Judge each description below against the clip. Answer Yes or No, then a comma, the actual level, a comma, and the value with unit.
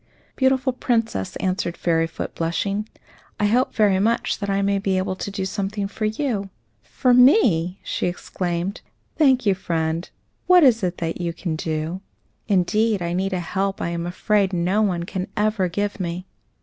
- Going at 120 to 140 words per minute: No, average, 165 wpm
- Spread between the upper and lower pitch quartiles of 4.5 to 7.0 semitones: No, average, 3.5 semitones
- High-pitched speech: Yes, high, 195 Hz